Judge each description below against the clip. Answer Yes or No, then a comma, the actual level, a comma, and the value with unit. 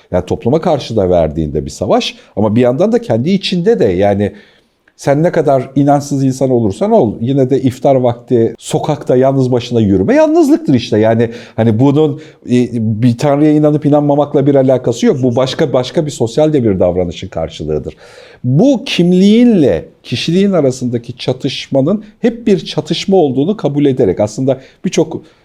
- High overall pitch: No, low, 135 Hz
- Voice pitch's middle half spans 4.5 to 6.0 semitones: Yes, average, 5.3 semitones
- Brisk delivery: Yes, fast, 155 wpm